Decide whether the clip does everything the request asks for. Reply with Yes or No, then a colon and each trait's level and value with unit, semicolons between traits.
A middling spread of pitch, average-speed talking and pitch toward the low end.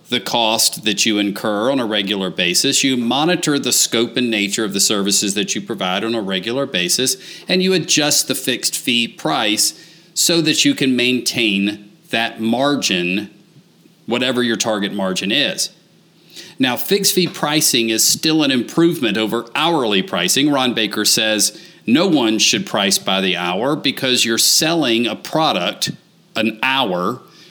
No: wide, 5.7 semitones; average, 155 wpm; low, 115 Hz